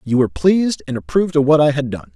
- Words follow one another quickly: Yes, fast, 280 wpm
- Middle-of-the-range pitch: Yes, medium, 155 Hz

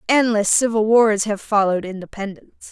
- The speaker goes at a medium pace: No, slow, 130 wpm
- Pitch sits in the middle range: No, high, 210 Hz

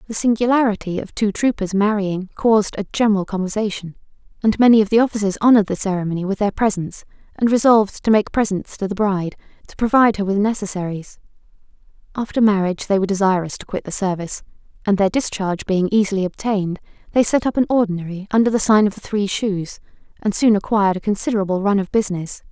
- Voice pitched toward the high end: Yes, high, 205 Hz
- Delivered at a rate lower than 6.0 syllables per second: No, 6.7 syllables/s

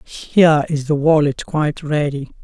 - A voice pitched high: No, medium, 150 Hz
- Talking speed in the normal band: Yes, average, 150 wpm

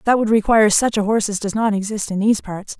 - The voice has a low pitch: No, high, 210 Hz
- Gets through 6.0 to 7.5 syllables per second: Yes, 6.8 syllables/s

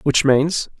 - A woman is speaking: No, male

